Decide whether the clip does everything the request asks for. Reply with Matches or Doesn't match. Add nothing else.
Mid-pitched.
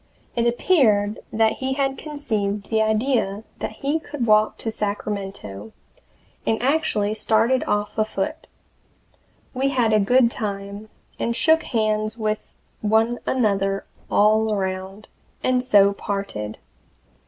Doesn't match